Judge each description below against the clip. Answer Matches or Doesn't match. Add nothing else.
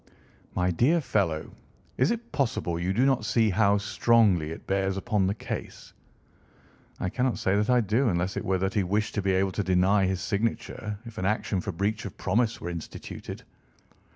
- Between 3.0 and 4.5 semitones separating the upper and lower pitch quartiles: Matches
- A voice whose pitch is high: Doesn't match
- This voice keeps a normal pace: Matches